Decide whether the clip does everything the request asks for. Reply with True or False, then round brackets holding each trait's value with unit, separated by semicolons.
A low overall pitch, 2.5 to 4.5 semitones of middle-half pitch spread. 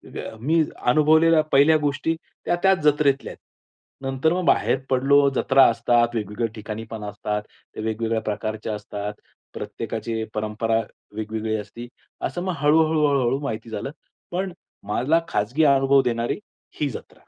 False (125 Hz; 5.2 semitones)